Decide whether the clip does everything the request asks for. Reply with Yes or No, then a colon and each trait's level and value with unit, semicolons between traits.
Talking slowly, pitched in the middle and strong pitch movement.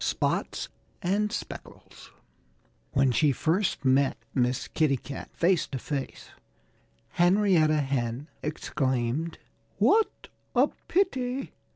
Yes: slow, 100 wpm; medium, 150 Hz; wide, 6.0 semitones